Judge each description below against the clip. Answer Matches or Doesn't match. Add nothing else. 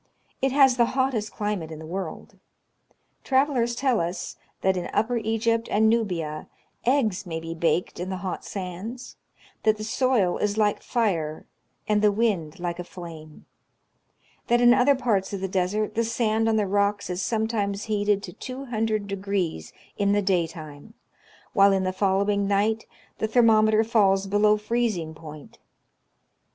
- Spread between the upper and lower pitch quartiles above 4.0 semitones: Doesn't match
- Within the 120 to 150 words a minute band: Doesn't match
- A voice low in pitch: Doesn't match